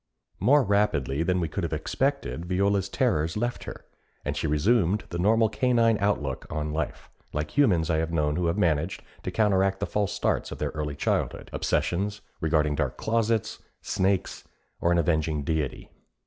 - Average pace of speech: Yes, average, 170 wpm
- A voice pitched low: Yes, very low, 90 Hz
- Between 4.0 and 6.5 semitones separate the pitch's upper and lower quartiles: Yes, average, 5.2 semitones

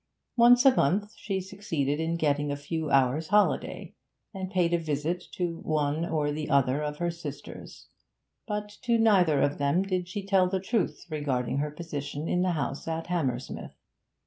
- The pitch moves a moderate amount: Yes, average, 4.5 semitones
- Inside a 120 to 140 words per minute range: No, average, 170 wpm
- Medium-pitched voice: Yes, medium, 165 Hz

